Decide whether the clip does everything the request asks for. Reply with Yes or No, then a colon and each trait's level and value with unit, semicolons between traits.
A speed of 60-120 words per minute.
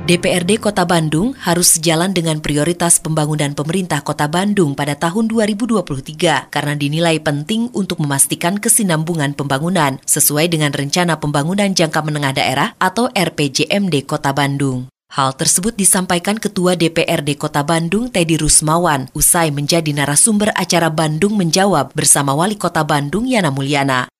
No: average, 130 wpm